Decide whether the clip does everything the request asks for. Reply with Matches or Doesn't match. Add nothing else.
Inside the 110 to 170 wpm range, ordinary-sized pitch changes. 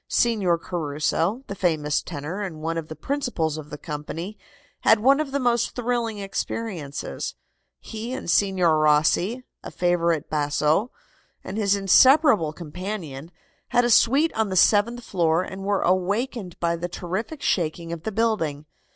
Doesn't match